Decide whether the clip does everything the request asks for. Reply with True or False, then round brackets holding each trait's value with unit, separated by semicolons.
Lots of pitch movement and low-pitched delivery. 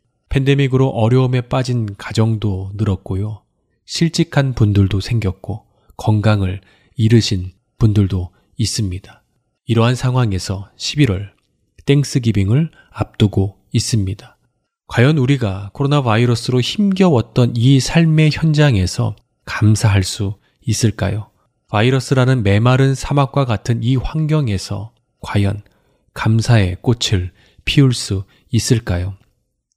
False (4.4 semitones; 115 Hz)